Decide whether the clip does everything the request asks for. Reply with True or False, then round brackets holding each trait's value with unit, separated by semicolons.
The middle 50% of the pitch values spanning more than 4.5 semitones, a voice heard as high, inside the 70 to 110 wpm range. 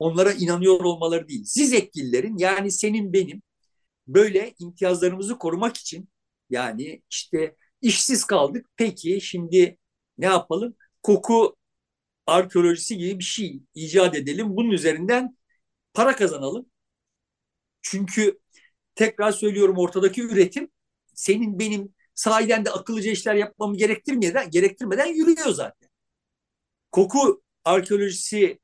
False (4.0 semitones; 200 Hz; 105 wpm)